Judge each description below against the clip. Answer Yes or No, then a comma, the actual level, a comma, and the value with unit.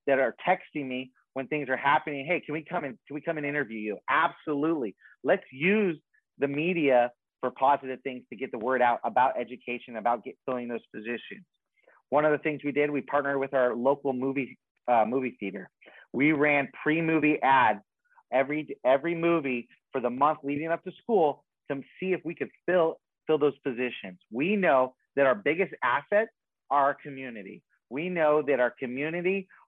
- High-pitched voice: No, medium, 140 Hz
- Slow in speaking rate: No, average, 185 wpm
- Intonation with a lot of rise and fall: No, average, 3.5 semitones